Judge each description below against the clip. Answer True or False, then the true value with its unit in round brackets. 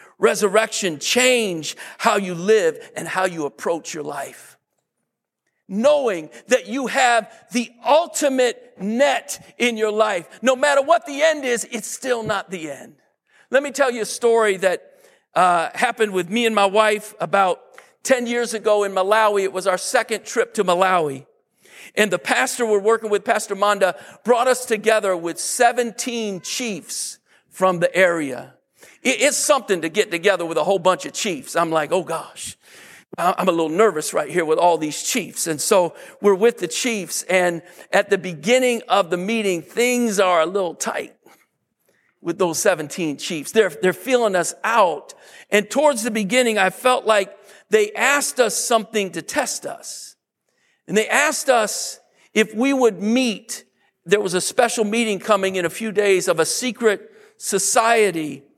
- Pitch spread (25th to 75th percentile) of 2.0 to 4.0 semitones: False (4.6 semitones)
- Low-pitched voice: False (215 Hz)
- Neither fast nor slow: True (170 wpm)